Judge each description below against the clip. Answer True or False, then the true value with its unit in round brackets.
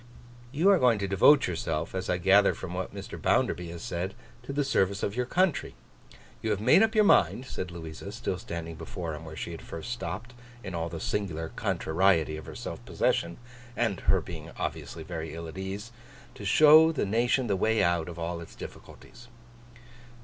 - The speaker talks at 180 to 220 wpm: True (190 wpm)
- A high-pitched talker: False (95 Hz)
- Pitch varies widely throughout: True (6.1 semitones)